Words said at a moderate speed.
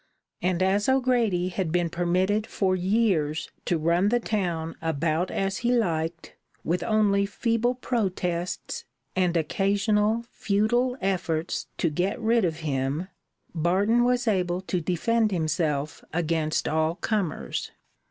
No: slow, 125 wpm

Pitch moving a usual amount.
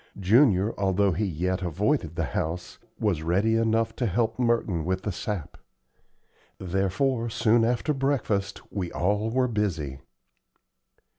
Yes: average, 4.0 semitones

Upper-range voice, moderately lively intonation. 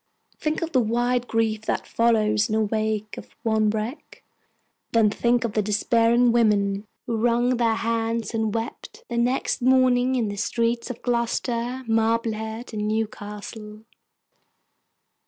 No: high, 230 Hz; narrow, 1.9 semitones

